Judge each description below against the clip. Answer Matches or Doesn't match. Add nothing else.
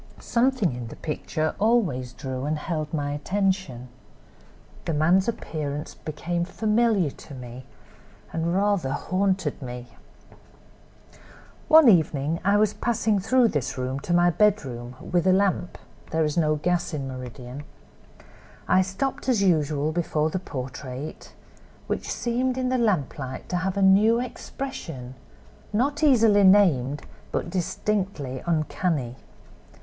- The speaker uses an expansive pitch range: Matches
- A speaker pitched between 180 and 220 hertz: Doesn't match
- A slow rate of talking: Matches